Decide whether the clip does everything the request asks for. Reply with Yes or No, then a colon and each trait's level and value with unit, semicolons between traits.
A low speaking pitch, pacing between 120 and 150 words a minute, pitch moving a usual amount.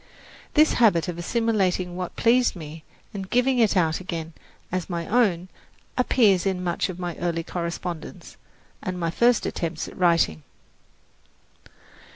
No: medium, 180 Hz; average, 140 wpm; average, 4.1 semitones